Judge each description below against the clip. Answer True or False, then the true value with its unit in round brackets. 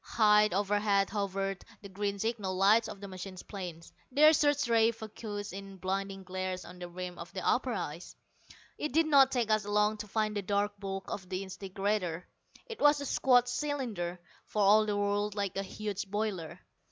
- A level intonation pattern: True (2.2 semitones)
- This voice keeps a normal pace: True (185 wpm)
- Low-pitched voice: False (205 Hz)